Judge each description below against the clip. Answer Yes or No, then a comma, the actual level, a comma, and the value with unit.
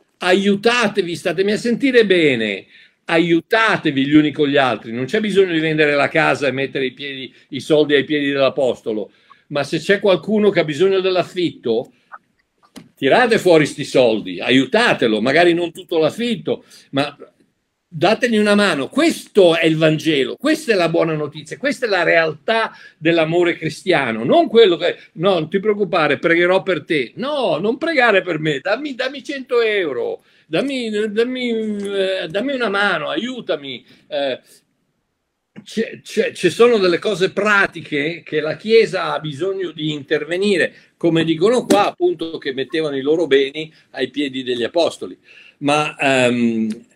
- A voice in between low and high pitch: Yes, medium, 175 Hz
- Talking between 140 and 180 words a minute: Yes, average, 150 wpm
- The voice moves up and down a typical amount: No, wide, 6.1 semitones